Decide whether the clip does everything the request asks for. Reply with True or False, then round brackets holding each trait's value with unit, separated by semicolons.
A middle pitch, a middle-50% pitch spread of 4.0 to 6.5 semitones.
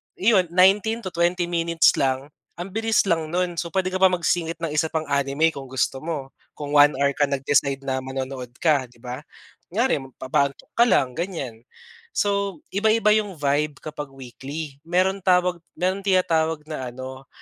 True (160 Hz; 5.0 semitones)